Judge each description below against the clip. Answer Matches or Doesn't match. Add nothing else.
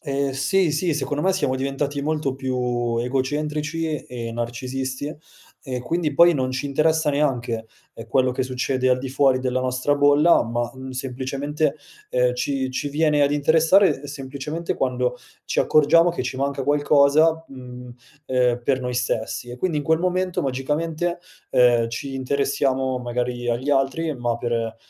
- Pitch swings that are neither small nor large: Matches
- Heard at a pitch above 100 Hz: Matches